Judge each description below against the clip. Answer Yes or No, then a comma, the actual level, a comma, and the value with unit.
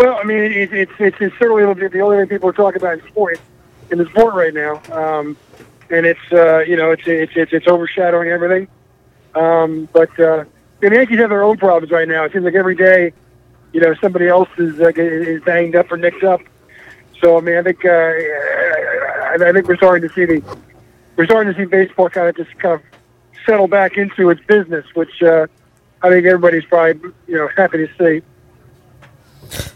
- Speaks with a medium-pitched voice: Yes, medium, 170 Hz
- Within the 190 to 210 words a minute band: Yes, fast, 205 wpm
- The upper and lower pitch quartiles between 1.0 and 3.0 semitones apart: Yes, narrow, 2.6 semitones